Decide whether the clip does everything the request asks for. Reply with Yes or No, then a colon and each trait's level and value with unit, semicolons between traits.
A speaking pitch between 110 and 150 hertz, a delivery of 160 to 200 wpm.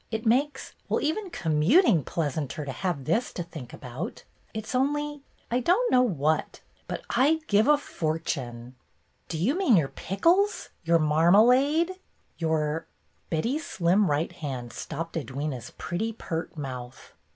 No: medium, 175 Hz; average, 165 wpm